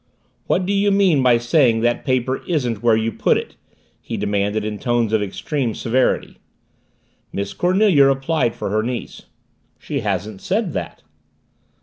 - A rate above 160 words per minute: No, average, 150 wpm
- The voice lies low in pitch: Yes, low, 120 Hz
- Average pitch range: No, wide, 5.7 semitones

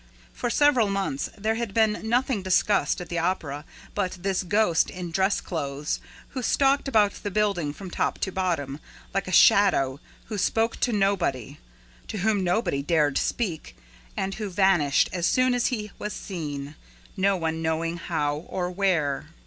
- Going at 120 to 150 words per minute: No, average, 165 wpm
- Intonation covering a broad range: No, average, 4.5 semitones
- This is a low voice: No, high, 190 Hz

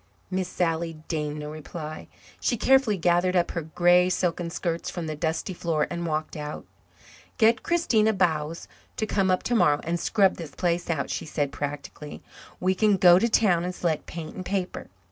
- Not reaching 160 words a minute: No, average, 180 wpm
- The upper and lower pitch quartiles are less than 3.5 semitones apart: Yes, average, 3.1 semitones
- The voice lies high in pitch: No, medium, 175 Hz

